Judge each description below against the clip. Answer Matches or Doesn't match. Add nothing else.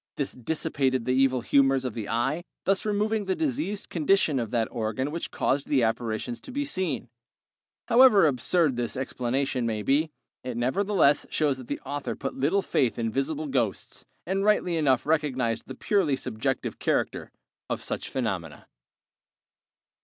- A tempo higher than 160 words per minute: Doesn't match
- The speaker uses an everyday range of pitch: Doesn't match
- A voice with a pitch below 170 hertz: Matches